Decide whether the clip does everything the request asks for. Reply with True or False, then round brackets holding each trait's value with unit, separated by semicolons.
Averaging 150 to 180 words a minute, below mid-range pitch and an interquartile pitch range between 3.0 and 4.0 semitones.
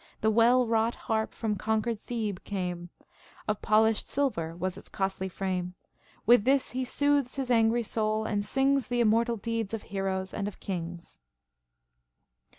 False (155 wpm; 220 Hz; 3.6 semitones)